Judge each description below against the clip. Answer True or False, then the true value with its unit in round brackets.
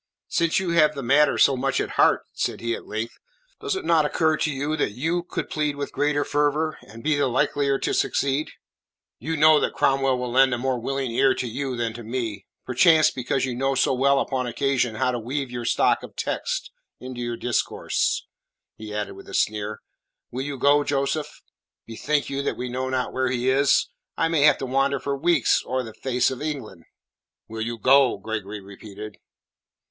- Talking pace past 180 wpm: True (200 wpm)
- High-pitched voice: False (135 Hz)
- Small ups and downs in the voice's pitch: False (3.3 semitones)